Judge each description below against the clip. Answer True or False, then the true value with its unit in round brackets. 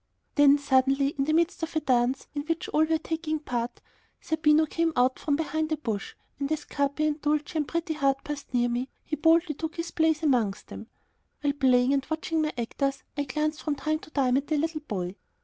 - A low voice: False (295 Hz)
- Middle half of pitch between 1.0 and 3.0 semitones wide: True (2.6 semitones)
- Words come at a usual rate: False (215 wpm)